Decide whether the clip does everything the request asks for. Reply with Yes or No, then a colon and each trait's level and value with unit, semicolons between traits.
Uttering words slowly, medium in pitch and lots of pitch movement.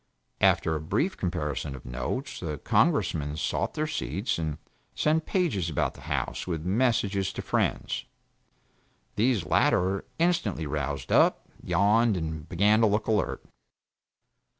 No: slow, 130 wpm; very low, 95 Hz; wide, 6.5 semitones